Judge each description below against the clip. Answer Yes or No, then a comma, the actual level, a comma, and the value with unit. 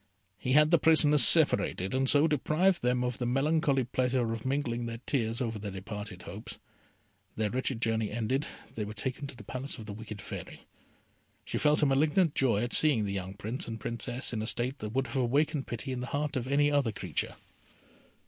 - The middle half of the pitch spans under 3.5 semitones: No, average, 4.1 semitones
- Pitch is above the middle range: No, low, 125 Hz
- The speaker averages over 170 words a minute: Yes, fast, 205 wpm